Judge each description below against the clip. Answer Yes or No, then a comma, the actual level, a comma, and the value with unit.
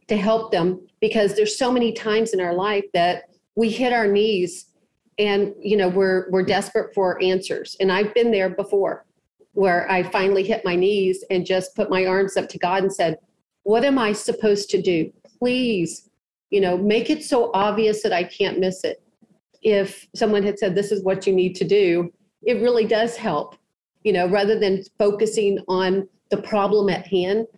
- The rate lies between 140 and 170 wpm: No, average, 190 wpm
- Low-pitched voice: No, high, 200 Hz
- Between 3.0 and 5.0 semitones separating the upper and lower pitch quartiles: No, narrow, 2.6 semitones